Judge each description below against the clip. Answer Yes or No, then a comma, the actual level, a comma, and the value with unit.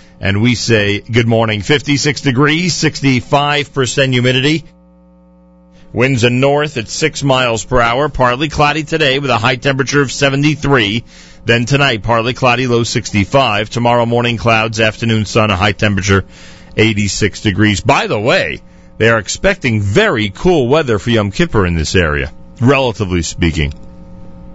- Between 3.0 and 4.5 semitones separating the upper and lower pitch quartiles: No, average, 5.1 semitones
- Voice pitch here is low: Yes, low, 115 Hz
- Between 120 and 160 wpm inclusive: Yes, average, 145 wpm